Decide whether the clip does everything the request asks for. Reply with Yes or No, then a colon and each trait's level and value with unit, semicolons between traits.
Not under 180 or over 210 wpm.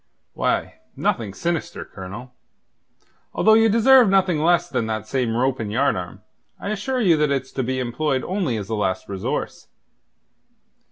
No: average, 155 wpm